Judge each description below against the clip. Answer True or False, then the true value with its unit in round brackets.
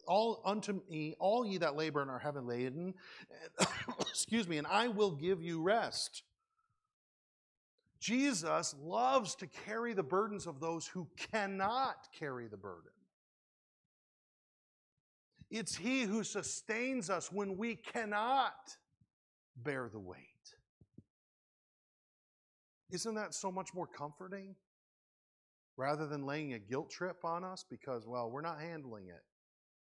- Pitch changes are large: True (6.1 semitones)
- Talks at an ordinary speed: False (125 wpm)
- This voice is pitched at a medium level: True (180 Hz)